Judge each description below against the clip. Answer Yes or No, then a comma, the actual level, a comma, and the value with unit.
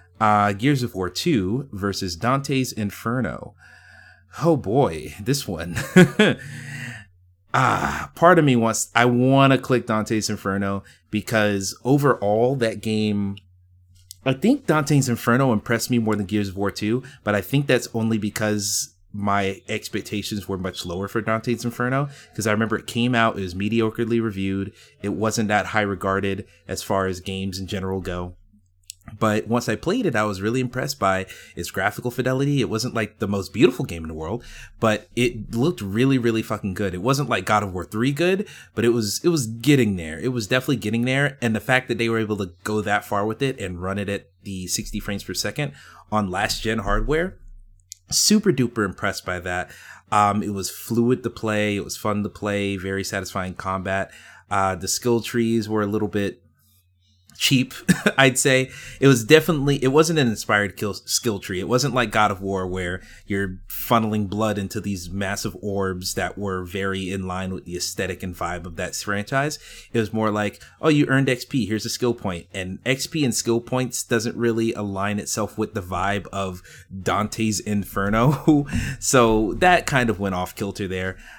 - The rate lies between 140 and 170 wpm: No, average, 185 wpm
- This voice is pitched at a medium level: No, low, 105 Hz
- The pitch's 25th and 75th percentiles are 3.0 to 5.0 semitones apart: Yes, average, 4.0 semitones